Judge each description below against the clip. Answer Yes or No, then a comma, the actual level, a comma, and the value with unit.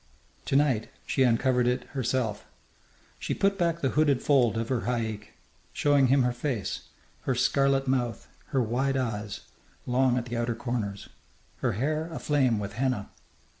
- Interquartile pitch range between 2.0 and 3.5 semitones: Yes, average, 3.0 semitones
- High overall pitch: No, low, 125 Hz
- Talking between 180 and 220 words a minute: No, average, 155 wpm